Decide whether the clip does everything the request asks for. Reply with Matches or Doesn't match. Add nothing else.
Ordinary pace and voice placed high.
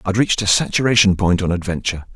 Doesn't match